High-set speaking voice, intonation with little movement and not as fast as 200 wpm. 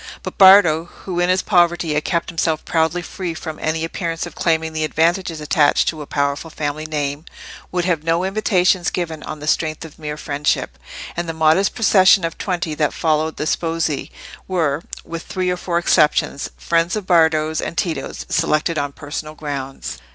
No: medium, 160 Hz; narrow, 2.2 semitones; average, 180 wpm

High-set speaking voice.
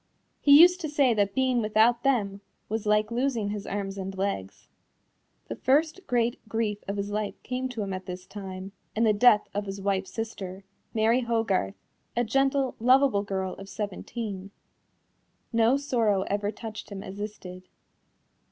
Yes: high, 210 Hz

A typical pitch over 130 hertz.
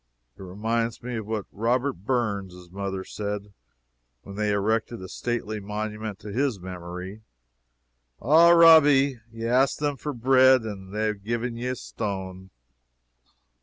No: low, 110 Hz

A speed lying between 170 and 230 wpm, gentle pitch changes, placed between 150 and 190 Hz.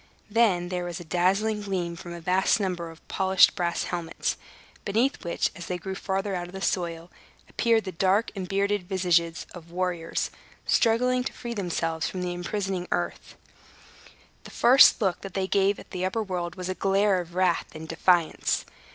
Yes: average, 180 wpm; narrow, 2.2 semitones; medium, 185 Hz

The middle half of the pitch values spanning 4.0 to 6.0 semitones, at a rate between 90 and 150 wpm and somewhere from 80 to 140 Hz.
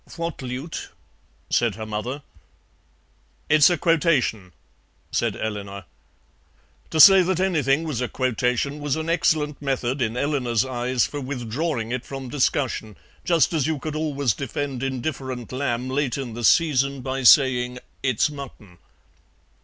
No: average, 3.5 semitones; average, 140 wpm; low, 135 Hz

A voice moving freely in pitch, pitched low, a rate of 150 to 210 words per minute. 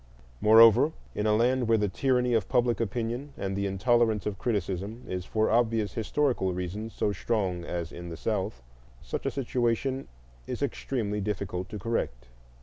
No: average, 3.7 semitones; low, 110 Hz; average, 160 wpm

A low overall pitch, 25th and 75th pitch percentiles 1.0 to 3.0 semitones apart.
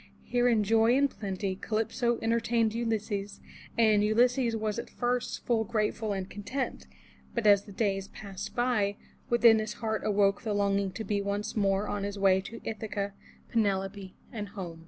No: high, 210 Hz; narrow, 2.4 semitones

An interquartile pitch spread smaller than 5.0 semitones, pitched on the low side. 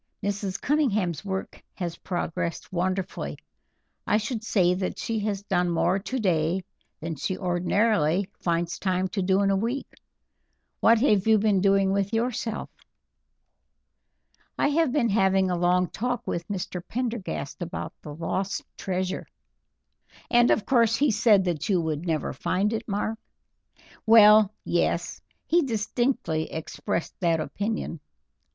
No: average, 3.7 semitones; high, 195 Hz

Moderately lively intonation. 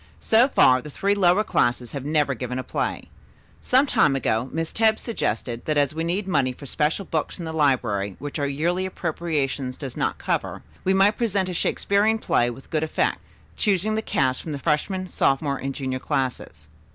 No: wide, 6.2 semitones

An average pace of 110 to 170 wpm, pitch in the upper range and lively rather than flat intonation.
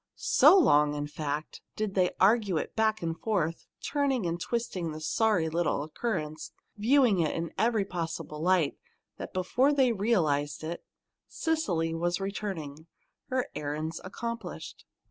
No: average, 140 wpm; medium, 180 Hz; wide, 5.9 semitones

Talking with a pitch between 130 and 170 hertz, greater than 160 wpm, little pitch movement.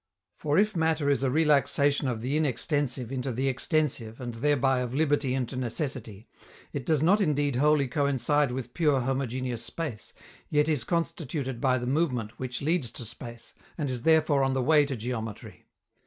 No: low, 135 Hz; average, 170 wpm; average, 3.2 semitones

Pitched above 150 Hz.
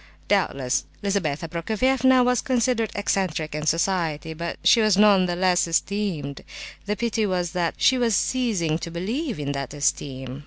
Yes: medium, 185 Hz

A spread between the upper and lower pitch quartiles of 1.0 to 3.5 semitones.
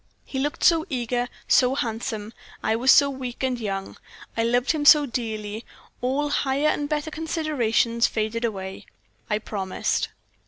No: average, 4.4 semitones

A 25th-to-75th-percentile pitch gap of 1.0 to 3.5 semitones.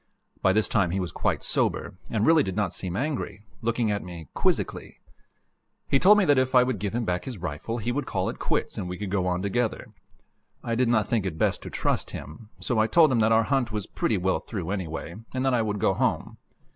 No: average, 4.6 semitones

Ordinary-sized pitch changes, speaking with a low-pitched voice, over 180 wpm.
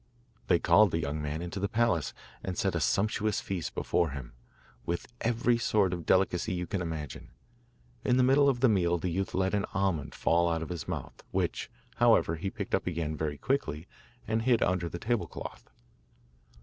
Yes: average, 4.6 semitones; very low, 90 Hz; average, 190 wpm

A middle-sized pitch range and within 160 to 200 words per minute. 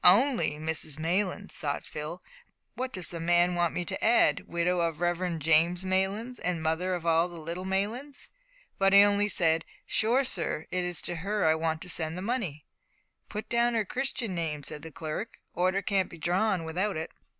Yes: average, 3.6 semitones; average, 185 wpm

